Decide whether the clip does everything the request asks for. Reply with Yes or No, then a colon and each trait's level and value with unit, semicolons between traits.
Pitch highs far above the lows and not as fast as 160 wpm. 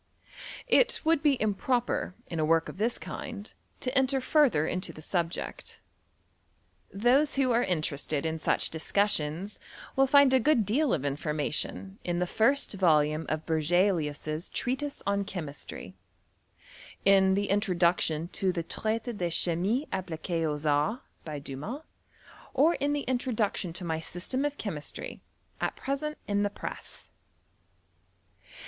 Yes: wide, 7.8 semitones; average, 140 wpm